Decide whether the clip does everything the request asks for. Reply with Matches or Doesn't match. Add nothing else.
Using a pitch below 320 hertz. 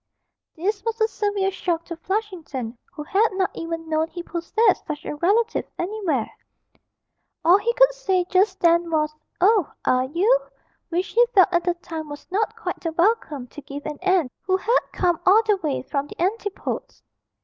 Doesn't match